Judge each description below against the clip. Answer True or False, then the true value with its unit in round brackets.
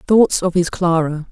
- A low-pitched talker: False (175 Hz)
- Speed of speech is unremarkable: True (180 wpm)